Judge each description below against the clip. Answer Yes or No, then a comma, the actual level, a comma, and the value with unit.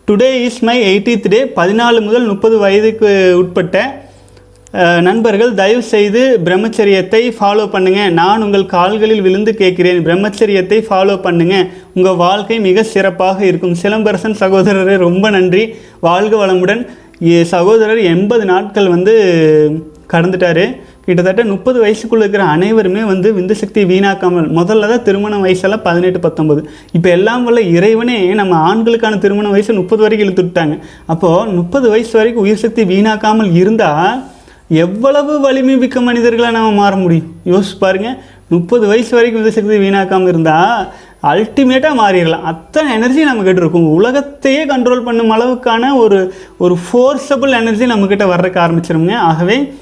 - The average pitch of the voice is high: Yes, high, 200 Hz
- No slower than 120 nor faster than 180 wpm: Yes, fast, 130 wpm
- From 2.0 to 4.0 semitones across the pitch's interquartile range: Yes, average, 3.7 semitones